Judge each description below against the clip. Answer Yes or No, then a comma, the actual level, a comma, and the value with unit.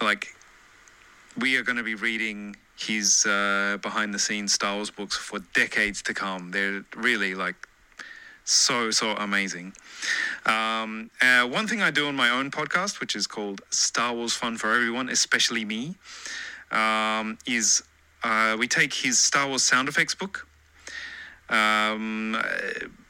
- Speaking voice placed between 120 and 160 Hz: No, low, 110 Hz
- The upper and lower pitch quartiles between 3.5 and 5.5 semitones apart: No, average, 2.8 semitones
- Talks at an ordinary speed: Yes, average, 150 wpm